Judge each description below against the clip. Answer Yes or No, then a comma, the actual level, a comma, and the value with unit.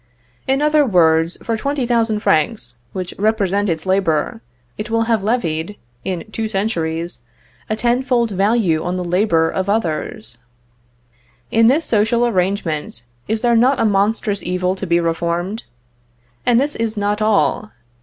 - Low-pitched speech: No, high, 205 Hz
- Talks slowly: No, average, 145 wpm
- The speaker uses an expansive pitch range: No, average, 4.8 semitones